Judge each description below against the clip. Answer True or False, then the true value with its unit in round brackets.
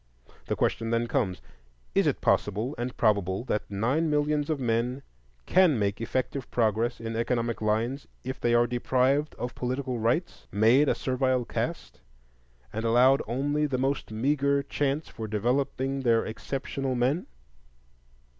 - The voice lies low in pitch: True (125 Hz)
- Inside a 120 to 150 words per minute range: True (145 wpm)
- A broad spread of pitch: False (3.3 semitones)